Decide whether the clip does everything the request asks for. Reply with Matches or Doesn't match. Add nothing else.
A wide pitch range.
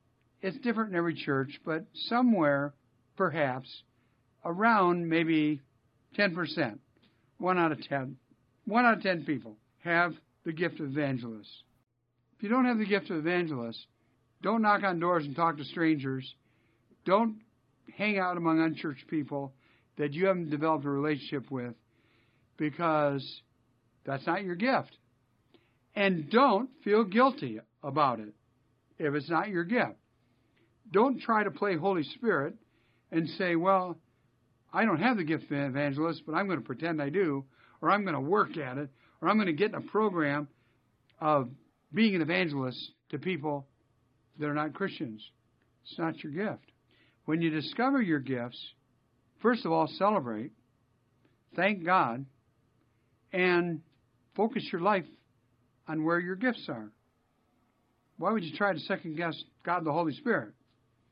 Matches